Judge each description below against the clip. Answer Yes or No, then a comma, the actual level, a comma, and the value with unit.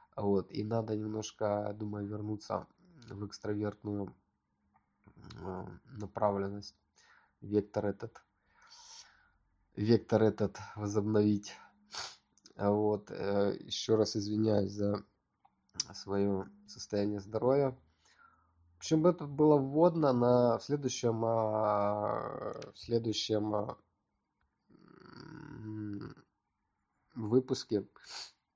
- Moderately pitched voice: No, low, 105 Hz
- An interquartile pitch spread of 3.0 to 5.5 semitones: No, narrow, 2.4 semitones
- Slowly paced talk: Yes, slow, 65 wpm